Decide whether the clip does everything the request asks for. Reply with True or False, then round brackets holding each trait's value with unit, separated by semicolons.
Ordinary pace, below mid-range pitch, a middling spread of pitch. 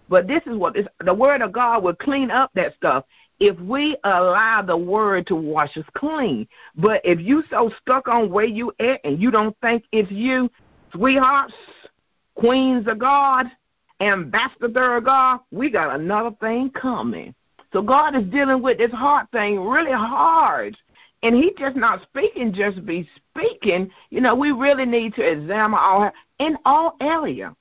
False (170 wpm; 235 Hz; 4.1 semitones)